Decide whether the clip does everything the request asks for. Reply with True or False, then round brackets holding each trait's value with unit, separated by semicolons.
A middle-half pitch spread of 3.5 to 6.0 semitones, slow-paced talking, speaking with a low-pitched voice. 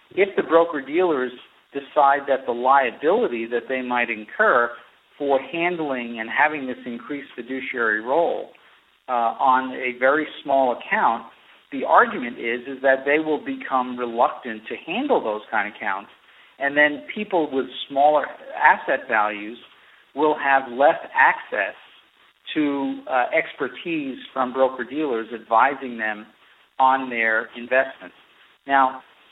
False (2.9 semitones; 125 wpm; 130 Hz)